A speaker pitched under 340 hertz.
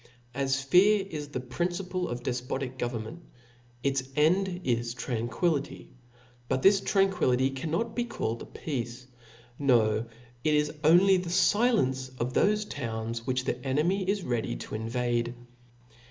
Yes: low, 135 Hz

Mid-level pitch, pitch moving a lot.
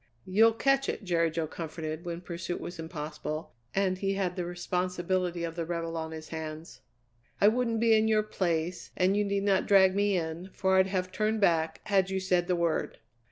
No: medium, 180 Hz; average, 2.9 semitones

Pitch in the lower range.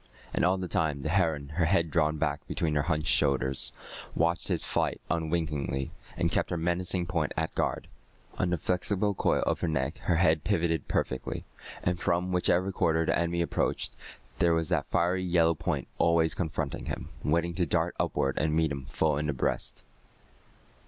Yes: very low, 80 Hz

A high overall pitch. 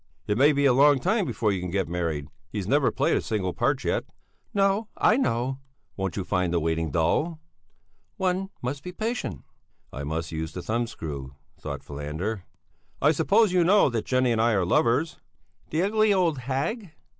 No: low, 120 Hz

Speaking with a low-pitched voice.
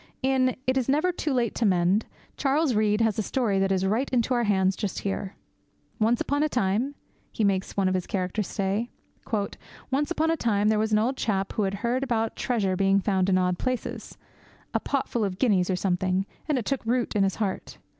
No: high, 215 Hz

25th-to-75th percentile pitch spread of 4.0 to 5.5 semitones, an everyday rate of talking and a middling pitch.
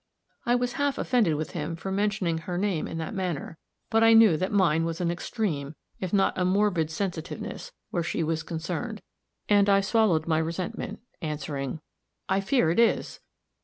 Yes: average, 4.3 semitones; average, 175 wpm; medium, 180 Hz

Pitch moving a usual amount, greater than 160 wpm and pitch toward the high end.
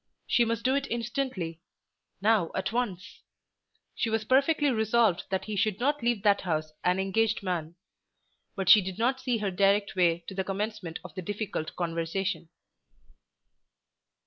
No: average, 4.1 semitones; average, 155 wpm; high, 200 Hz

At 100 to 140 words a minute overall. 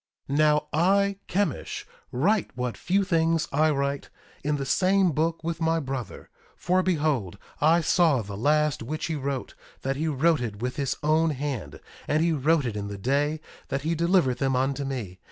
No: average, 185 wpm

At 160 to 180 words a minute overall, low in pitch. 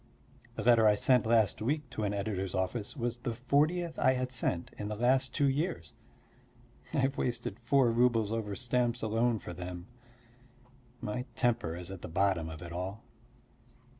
Yes: average, 170 wpm; low, 115 Hz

